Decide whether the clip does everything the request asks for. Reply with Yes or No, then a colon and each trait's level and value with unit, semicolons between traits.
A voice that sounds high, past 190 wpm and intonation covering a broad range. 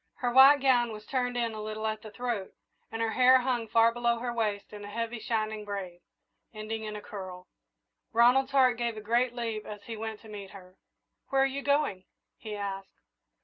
No: high, 225 Hz; fast, 205 wpm; narrow, 2.6 semitones